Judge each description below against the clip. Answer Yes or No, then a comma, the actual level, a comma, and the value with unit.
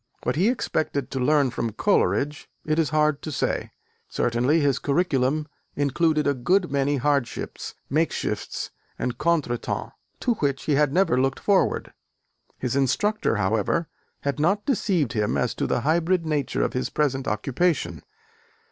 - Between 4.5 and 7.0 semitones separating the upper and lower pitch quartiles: No, average, 3.9 semitones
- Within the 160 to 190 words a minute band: No, average, 145 wpm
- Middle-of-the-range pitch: Yes, medium, 145 Hz